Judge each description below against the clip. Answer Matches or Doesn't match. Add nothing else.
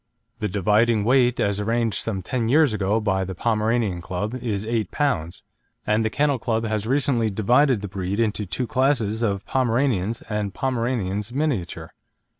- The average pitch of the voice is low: Matches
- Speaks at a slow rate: Doesn't match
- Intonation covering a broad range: Doesn't match